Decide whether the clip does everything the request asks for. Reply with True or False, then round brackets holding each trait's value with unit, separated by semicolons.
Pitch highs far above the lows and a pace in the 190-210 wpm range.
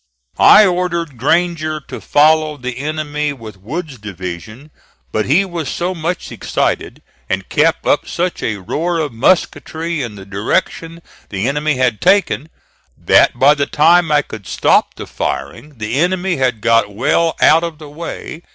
False (6.2 semitones; 160 wpm)